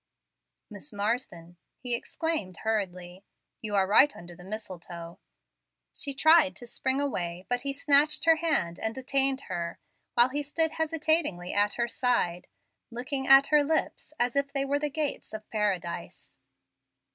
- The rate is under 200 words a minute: Yes, average, 150 wpm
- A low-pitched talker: No, high, 245 Hz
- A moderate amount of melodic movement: No, wide, 7.0 semitones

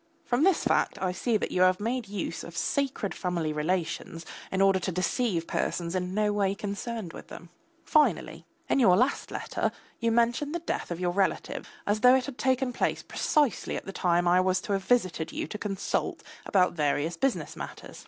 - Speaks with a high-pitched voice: Yes, high, 195 Hz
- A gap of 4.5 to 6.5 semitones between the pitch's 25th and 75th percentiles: Yes, average, 5.1 semitones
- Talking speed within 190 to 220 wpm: Yes, average, 200 wpm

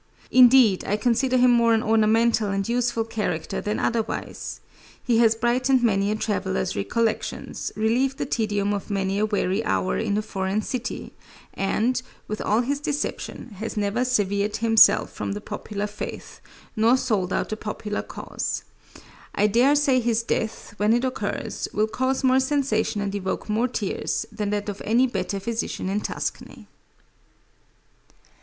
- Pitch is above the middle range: Yes, high, 220 Hz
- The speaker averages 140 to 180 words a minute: Yes, average, 155 wpm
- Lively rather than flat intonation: No, average, 2.9 semitones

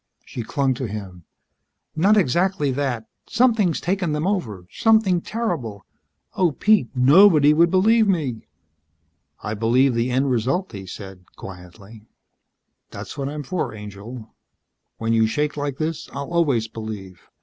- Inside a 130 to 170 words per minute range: Yes, average, 140 wpm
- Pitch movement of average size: No, wide, 7.7 semitones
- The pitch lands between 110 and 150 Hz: Yes, low, 135 Hz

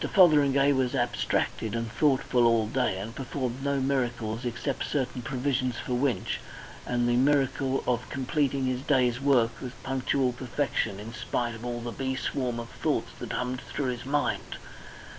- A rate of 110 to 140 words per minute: No, average, 165 wpm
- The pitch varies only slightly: Yes, narrow, 2.3 semitones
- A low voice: Yes, low, 125 Hz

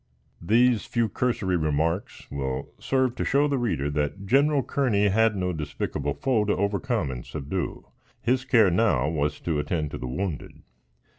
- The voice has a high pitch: No, very low, 95 Hz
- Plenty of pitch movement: Yes, wide, 8.1 semitones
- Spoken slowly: No, average, 160 wpm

